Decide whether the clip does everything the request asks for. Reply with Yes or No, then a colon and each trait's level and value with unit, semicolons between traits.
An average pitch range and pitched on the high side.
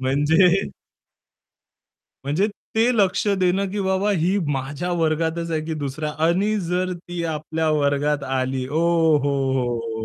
No: average, 4.2 semitones; medium, 160 Hz